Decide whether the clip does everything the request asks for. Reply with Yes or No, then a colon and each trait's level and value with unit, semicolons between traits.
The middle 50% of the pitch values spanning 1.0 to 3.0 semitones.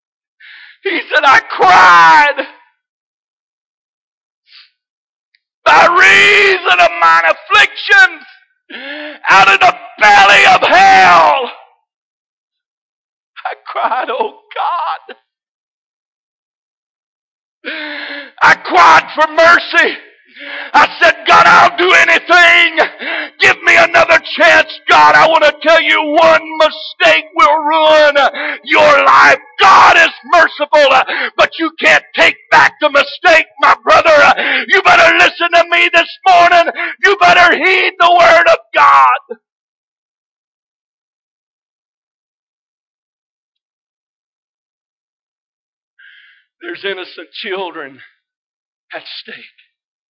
No: average, 3.6 semitones